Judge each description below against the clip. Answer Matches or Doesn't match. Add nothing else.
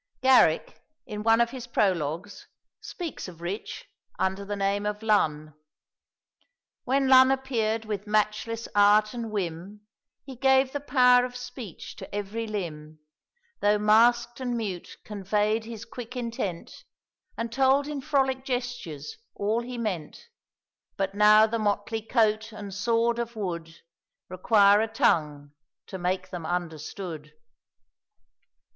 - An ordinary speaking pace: Doesn't match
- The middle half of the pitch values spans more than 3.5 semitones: Matches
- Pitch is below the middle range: Doesn't match